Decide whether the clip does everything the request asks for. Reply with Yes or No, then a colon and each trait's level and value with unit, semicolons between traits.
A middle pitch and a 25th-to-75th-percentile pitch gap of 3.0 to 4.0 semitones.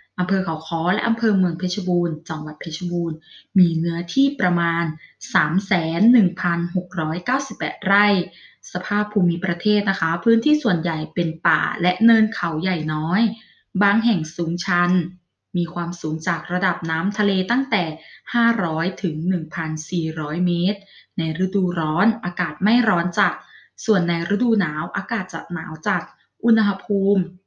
Yes: medium, 180 Hz; average, 3.4 semitones